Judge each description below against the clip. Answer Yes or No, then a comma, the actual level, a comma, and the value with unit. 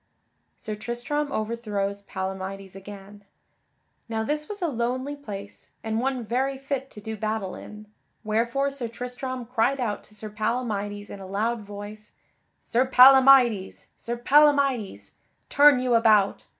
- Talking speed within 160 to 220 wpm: No, average, 140 wpm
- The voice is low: No, high, 230 Hz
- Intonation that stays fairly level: No, average, 4.1 semitones